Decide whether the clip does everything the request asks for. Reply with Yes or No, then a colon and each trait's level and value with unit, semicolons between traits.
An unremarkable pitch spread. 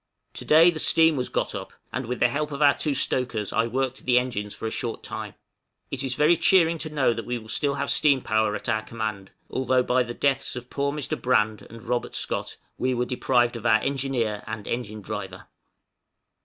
Yes: average, 3.7 semitones